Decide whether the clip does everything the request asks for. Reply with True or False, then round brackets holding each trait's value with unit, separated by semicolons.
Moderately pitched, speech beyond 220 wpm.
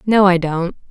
False (180 Hz; 200 wpm)